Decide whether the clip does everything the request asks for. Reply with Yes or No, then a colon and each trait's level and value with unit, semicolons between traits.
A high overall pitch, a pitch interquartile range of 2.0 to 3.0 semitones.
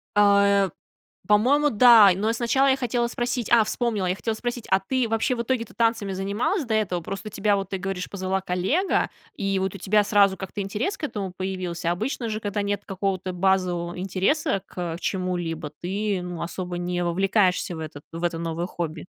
No: high, 195 Hz; average, 3.6 semitones